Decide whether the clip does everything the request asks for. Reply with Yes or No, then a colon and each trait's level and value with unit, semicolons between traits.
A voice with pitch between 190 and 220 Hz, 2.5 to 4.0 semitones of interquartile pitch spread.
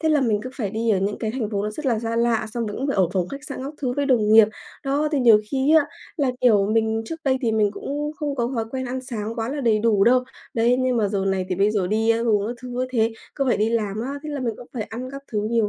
No: high, 230 Hz; average, 3.6 semitones